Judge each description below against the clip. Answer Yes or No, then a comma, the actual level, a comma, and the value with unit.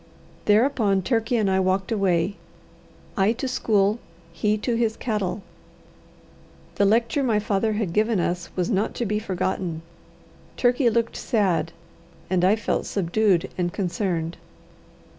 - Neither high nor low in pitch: No, high, 205 Hz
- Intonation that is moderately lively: Yes, average, 3.3 semitones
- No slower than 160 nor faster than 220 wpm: No, slow, 135 wpm